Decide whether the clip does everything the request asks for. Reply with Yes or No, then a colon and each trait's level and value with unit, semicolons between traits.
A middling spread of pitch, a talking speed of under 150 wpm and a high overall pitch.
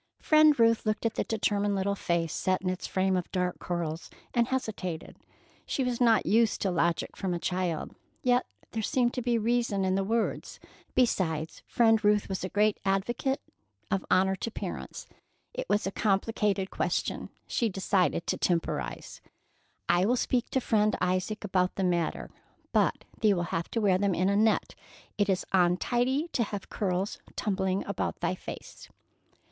No: average, 3.7 semitones; average, 170 wpm; high, 200 Hz